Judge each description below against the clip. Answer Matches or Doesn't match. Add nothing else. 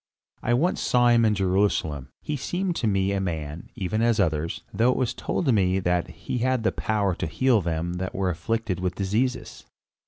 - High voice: Doesn't match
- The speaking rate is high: Doesn't match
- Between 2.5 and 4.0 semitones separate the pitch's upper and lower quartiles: Doesn't match